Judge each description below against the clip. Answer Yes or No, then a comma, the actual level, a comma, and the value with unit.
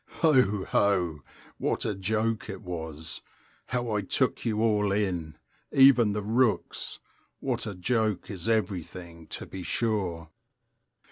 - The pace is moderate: No, slow, 130 wpm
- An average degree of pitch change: Yes, average, 3.9 semitones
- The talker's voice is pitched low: Yes, low, 105 Hz